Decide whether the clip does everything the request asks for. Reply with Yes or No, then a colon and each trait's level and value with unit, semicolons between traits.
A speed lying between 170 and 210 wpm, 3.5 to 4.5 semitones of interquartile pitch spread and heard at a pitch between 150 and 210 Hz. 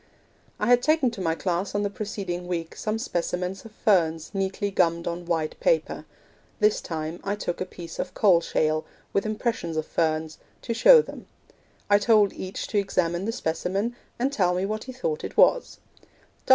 Yes: average, 180 wpm; average, 4.1 semitones; high, 190 Hz